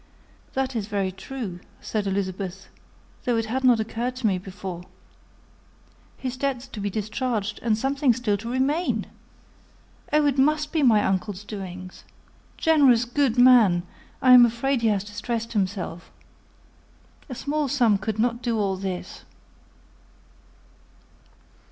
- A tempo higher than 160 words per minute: No, slow, 135 wpm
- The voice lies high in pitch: Yes, high, 225 Hz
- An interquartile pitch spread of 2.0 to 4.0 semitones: No, average, 4.5 semitones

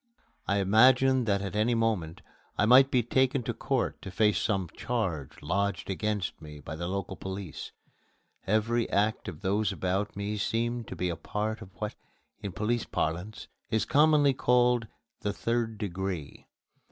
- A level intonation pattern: No, average, 3.7 semitones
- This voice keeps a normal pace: Yes, average, 160 wpm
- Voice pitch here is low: Yes, low, 105 Hz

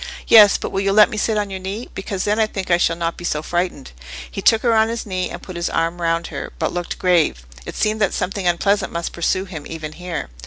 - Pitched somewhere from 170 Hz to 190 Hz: Yes, medium, 185 Hz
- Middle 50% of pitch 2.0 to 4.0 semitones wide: Yes, average, 3.4 semitones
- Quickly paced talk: Yes, fast, 260 wpm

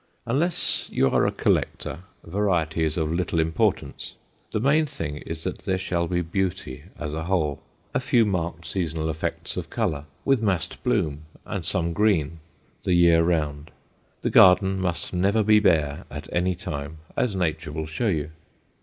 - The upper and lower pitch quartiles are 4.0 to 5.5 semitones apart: No, average, 3.4 semitones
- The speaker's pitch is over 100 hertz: No, very low, 85 Hz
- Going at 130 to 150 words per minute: No, average, 165 wpm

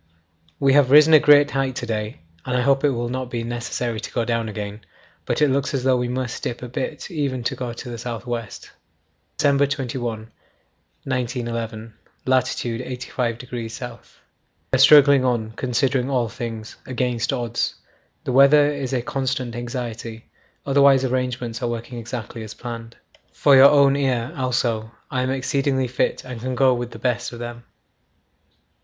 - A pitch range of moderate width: No, narrow, 2.2 semitones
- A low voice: Yes, low, 125 Hz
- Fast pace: No, average, 170 wpm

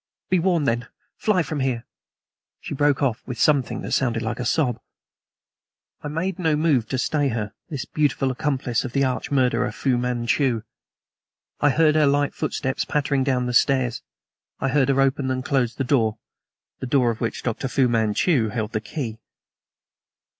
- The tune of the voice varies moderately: Yes, average, 3.2 semitones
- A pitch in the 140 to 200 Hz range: No, low, 130 Hz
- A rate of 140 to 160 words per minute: No, average, 175 wpm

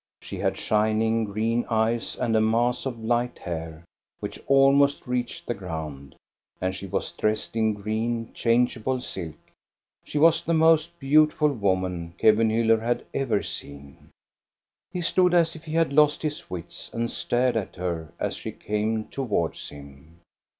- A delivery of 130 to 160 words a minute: Yes, average, 150 wpm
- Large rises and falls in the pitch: Yes, wide, 5.8 semitones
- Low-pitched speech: Yes, low, 115 Hz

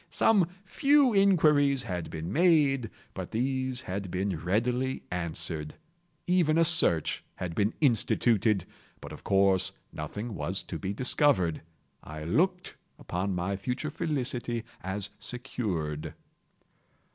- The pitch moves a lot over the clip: Yes, wide, 7.8 semitones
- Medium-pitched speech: No, low, 115 Hz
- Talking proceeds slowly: Yes, slow, 115 wpm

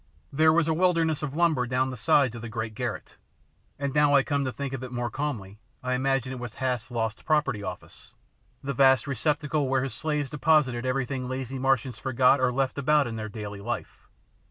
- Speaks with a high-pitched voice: No, low, 130 Hz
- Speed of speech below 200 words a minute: No, fast, 205 wpm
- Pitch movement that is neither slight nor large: Yes, average, 3.0 semitones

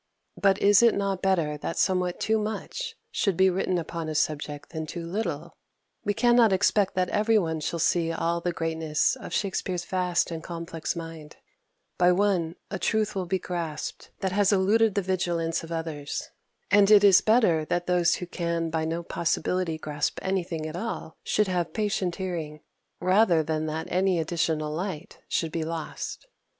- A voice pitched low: No, medium, 175 Hz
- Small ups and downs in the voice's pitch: No, average, 3.1 semitones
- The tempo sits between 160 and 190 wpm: Yes, average, 175 wpm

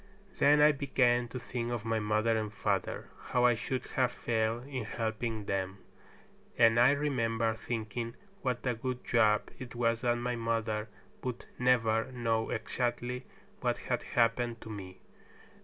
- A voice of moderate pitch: No, low, 115 Hz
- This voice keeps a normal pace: Yes, average, 155 wpm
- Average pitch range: No, narrow, 1.8 semitones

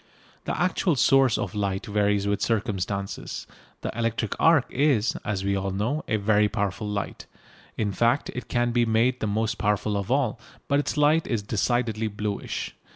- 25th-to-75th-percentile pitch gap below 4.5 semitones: Yes, average, 3.2 semitones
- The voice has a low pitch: Yes, low, 110 Hz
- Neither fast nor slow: Yes, average, 170 wpm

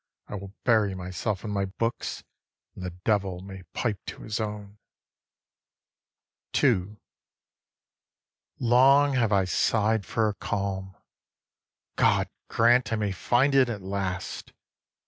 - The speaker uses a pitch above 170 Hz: No, low, 105 Hz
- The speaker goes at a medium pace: No, slow, 125 wpm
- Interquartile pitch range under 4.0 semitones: Yes, average, 3.1 semitones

